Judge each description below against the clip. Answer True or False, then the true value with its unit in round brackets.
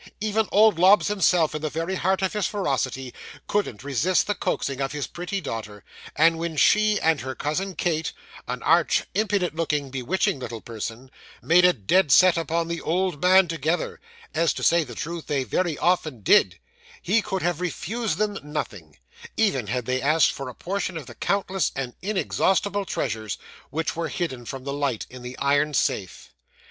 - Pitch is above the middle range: False (165 Hz)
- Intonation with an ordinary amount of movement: False (6.0 semitones)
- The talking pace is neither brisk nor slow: True (180 wpm)